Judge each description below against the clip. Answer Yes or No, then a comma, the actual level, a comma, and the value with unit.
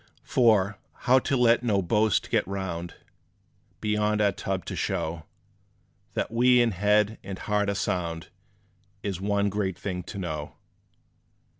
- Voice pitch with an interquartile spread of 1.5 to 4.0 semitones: Yes, narrow, 2.4 semitones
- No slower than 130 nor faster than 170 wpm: Yes, average, 140 wpm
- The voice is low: Yes, low, 100 Hz